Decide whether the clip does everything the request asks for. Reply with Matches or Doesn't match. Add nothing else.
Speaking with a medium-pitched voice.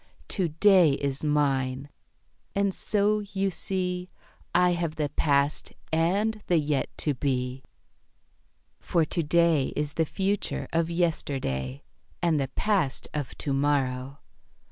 Matches